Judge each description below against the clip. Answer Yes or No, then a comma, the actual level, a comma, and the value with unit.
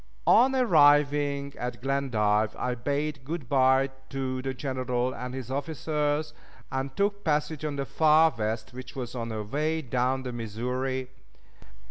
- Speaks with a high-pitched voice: No, low, 135 Hz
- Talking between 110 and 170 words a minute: Yes, average, 145 wpm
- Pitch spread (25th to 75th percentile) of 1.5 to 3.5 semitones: Yes, average, 2.8 semitones